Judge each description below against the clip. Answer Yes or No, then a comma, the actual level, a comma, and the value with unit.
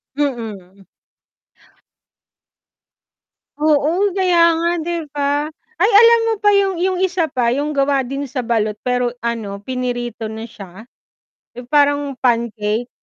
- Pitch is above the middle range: Yes, very high, 275 Hz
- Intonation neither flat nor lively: No, wide, 6.0 semitones